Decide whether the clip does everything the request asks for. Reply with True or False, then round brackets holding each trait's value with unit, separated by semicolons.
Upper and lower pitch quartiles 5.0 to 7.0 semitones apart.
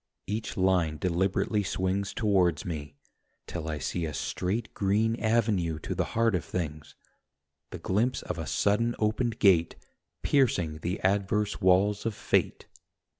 False (3.9 semitones)